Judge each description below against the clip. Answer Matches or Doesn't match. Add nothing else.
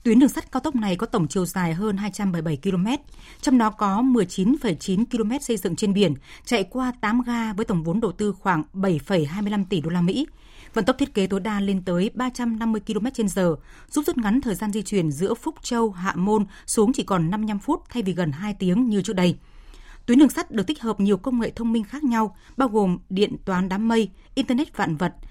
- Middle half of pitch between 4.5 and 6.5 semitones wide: Doesn't match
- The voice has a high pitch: Matches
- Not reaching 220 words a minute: Doesn't match